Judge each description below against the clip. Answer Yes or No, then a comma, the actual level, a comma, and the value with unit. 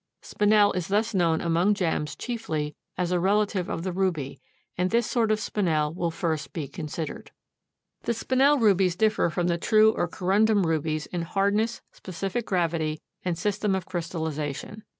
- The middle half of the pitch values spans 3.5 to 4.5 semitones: Yes, average, 4.2 semitones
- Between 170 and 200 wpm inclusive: No, average, 160 wpm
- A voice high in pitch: No, medium, 180 Hz